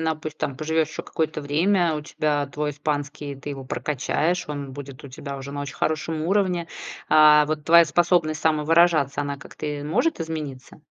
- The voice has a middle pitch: Yes, medium, 150 Hz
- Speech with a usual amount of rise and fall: No, narrow, 2.1 semitones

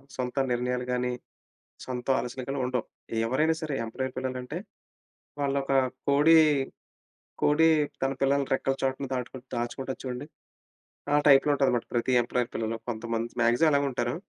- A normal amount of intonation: No, narrow, 2.2 semitones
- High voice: No, low, 130 Hz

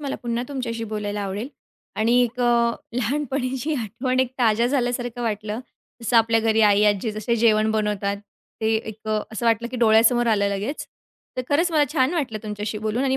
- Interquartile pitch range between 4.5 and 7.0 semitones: No, narrow, 2.6 semitones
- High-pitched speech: Yes, high, 230 Hz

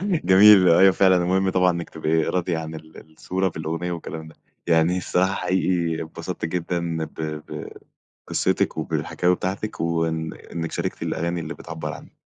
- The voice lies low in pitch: Yes, very low, 85 Hz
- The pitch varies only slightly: Yes, narrow, 2.3 semitones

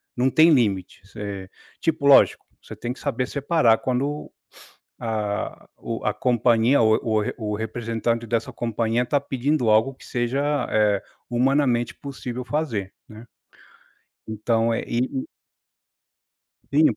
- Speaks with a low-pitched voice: Yes, low, 120 Hz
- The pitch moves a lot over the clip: No, average, 3.5 semitones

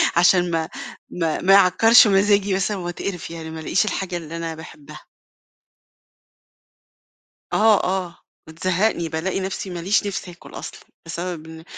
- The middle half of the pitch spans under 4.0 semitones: Yes, average, 2.8 semitones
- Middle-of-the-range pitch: Yes, medium, 180 Hz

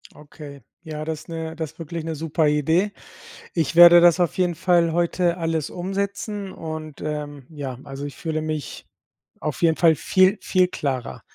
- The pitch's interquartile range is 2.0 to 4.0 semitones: Yes, narrow, 2.4 semitones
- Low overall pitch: No, medium, 160 Hz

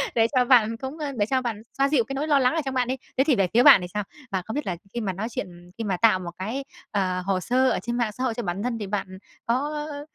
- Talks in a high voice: Yes, high, 235 Hz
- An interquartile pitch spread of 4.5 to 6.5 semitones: Yes, average, 4.9 semitones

